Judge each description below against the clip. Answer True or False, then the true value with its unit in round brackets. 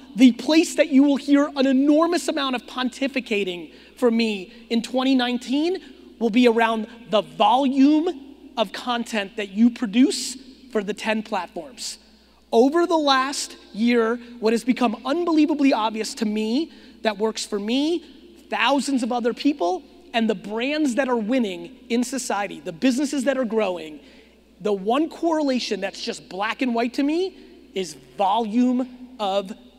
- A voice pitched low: False (250 Hz)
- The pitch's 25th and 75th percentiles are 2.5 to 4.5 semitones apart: True (4.1 semitones)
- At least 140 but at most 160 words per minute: True (150 wpm)